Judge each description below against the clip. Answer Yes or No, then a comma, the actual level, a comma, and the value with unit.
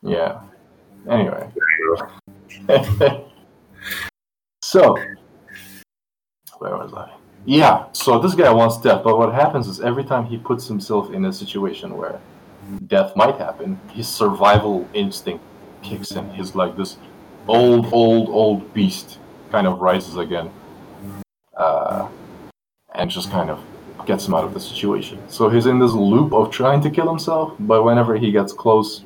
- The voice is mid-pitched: No, low, 115 Hz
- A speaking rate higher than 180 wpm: No, average, 145 wpm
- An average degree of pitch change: No, wide, 5.7 semitones